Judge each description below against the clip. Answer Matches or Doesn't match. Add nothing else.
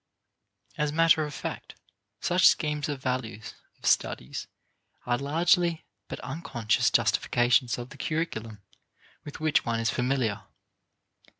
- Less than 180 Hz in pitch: Matches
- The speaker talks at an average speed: Doesn't match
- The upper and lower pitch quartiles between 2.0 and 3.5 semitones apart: Doesn't match